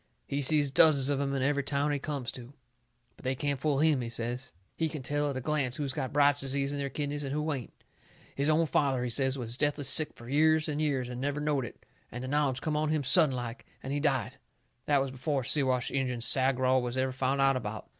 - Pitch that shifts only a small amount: Yes, narrow, 2.1 semitones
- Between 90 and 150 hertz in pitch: Yes, medium, 140 Hz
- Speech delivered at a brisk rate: Yes, fast, 240 wpm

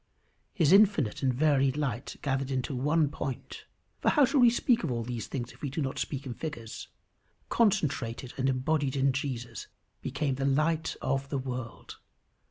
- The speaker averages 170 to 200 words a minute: Yes, average, 180 wpm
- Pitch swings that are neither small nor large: Yes, average, 3.1 semitones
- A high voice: No, low, 135 Hz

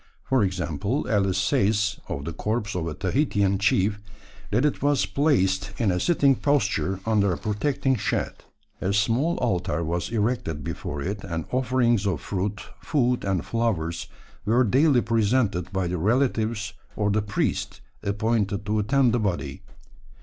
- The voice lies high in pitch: No, low, 105 Hz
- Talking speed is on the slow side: No, average, 150 wpm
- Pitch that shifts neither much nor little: Yes, average, 4.1 semitones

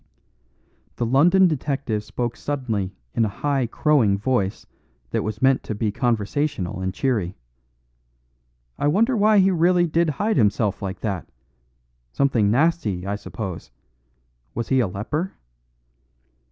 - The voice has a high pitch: No, low, 120 Hz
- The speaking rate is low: Yes, slow, 130 wpm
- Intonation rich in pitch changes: Yes, wide, 6.8 semitones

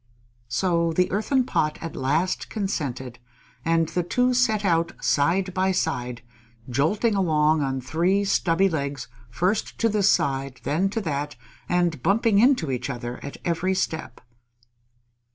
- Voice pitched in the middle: Yes, medium, 165 Hz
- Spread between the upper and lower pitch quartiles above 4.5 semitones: Yes, wide, 5.5 semitones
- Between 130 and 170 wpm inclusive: Yes, average, 140 wpm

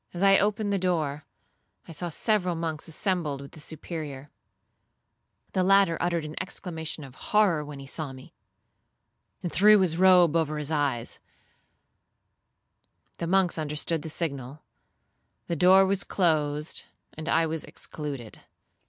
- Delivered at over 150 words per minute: No, average, 140 wpm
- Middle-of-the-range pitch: Yes, medium, 160 Hz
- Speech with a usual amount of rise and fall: Yes, average, 3.6 semitones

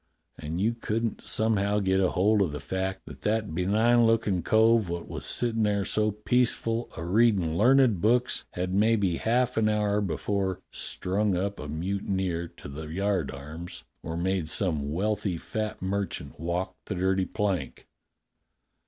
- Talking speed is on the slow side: No, average, 150 wpm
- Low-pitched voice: Yes, low, 100 Hz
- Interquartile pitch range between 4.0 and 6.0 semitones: No, average, 3.6 semitones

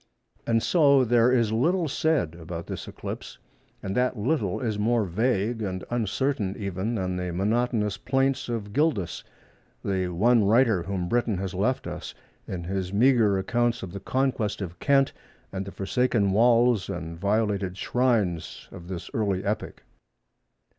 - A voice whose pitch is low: Yes, low, 105 Hz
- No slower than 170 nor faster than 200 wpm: No, average, 145 wpm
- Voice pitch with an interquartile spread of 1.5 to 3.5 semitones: No, average, 4.3 semitones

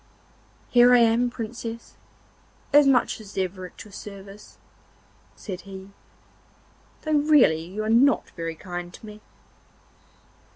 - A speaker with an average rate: No, slow, 125 wpm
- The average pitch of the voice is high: Yes, high, 215 Hz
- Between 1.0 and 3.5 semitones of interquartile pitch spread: No, average, 4.2 semitones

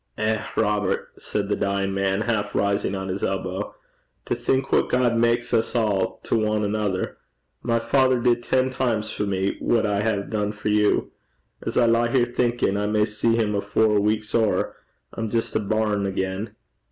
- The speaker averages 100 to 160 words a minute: No, average, 185 wpm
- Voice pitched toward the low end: Yes, low, 105 Hz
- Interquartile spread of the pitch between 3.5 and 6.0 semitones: No, narrow, 2.5 semitones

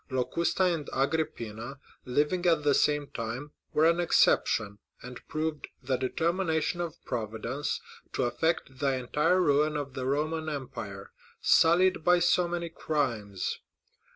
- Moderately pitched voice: Yes, medium, 145 Hz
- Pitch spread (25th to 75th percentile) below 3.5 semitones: No, average, 4.5 semitones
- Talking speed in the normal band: No, slow, 130 wpm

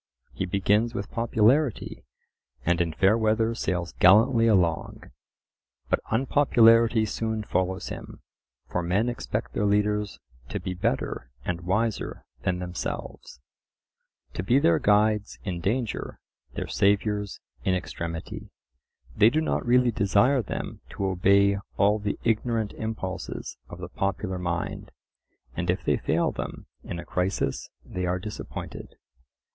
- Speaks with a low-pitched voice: Yes, low, 105 Hz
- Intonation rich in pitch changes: No, average, 3.6 semitones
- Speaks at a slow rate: Yes, slow, 130 wpm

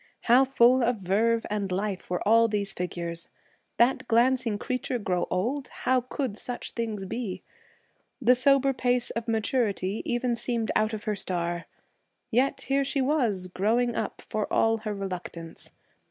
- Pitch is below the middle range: No, high, 225 Hz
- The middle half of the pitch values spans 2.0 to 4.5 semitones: Yes, average, 4.1 semitones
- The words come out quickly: No, average, 155 wpm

